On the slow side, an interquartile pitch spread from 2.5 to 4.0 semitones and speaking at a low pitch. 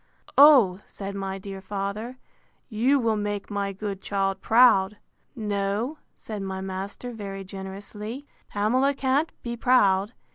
No: slow, 130 wpm; average, 3.5 semitones; high, 205 Hz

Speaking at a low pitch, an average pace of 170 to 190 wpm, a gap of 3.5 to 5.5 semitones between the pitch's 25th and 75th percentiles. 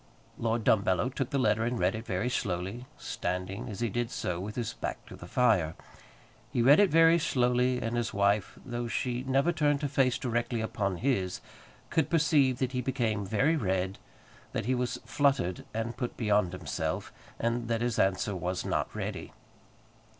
Yes: low, 120 Hz; average, 180 wpm; average, 4.4 semitones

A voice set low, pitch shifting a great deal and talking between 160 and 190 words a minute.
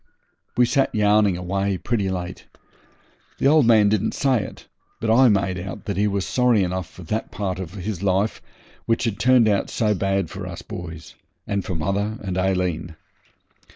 No: low, 100 Hz; average, 2.9 semitones; average, 180 wpm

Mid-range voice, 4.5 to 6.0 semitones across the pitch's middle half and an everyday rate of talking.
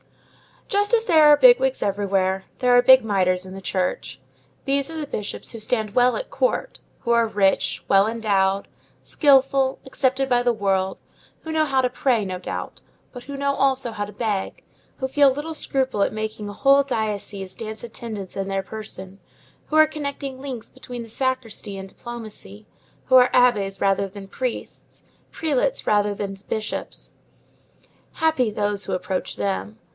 No: high, 225 Hz; wide, 5.4 semitones; average, 170 wpm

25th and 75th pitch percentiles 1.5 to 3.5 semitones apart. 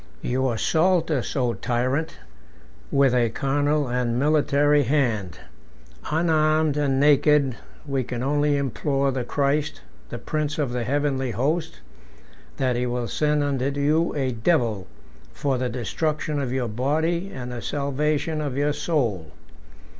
Yes: average, 3.2 semitones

